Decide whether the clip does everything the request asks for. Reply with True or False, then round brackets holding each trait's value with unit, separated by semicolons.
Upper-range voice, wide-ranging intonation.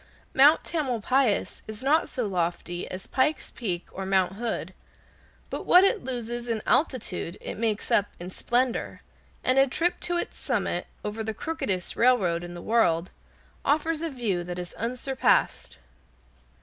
True (230 Hz; 6.2 semitones)